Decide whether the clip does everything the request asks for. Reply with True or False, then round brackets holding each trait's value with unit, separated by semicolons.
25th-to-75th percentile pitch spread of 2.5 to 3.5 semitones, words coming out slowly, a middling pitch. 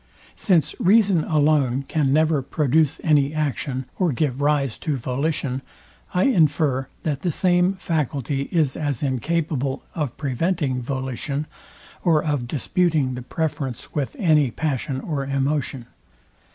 True (3.1 semitones; 125 wpm; 145 Hz)